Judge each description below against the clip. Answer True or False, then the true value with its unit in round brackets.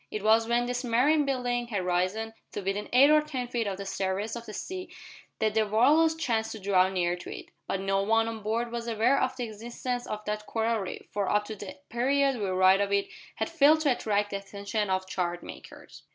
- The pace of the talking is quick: True (225 wpm)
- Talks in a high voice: True (220 Hz)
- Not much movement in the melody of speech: False (3.6 semitones)